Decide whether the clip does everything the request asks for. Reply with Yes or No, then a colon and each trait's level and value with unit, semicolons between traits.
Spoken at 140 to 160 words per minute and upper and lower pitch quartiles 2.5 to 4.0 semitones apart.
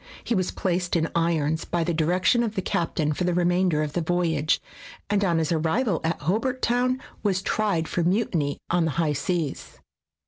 No: average, 185 wpm; average, 2.9 semitones